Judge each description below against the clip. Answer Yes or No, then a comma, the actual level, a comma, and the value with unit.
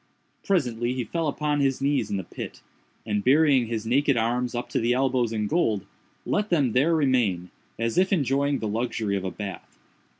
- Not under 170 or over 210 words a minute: Yes, average, 190 wpm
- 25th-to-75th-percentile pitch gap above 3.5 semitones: Yes, average, 4.1 semitones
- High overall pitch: No, low, 125 Hz